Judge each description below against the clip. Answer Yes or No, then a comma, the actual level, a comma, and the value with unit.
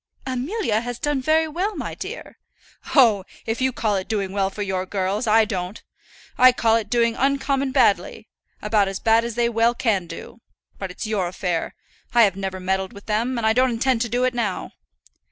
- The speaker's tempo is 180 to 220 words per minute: Yes, average, 195 wpm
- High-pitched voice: Yes, high, 225 Hz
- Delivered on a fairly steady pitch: No, average, 4.2 semitones